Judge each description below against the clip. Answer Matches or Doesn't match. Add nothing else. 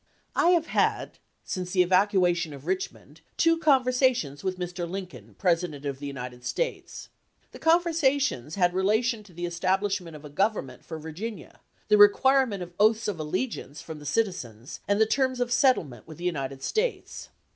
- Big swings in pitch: Matches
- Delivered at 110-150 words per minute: Doesn't match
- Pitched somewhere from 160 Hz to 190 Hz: Matches